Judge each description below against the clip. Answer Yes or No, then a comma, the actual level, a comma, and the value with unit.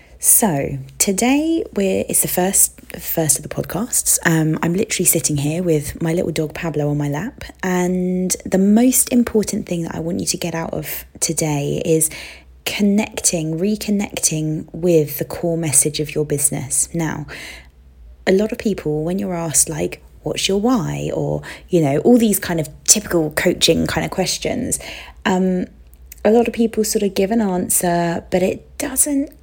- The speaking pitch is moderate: Yes, medium, 170 Hz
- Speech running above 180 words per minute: No, average, 170 wpm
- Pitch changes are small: No, average, 5.0 semitones